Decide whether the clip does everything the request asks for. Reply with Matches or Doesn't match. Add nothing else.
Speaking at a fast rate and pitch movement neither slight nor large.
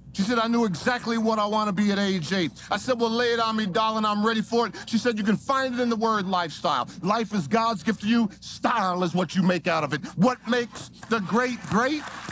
Matches